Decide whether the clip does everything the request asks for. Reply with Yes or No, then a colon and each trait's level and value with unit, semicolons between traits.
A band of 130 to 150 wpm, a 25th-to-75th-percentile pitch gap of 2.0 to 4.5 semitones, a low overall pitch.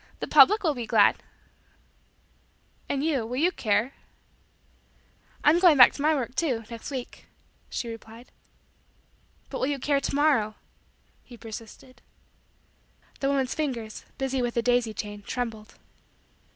No: average, 140 wpm; average, 3.8 semitones; very high, 250 Hz